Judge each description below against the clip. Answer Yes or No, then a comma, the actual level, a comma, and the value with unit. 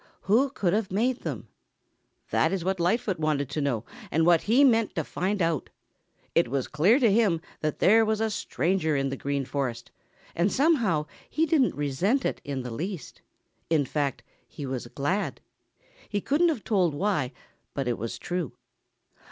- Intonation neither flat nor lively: No, wide, 7.2 semitones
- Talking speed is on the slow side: No, average, 175 wpm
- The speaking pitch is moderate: Yes, medium, 175 Hz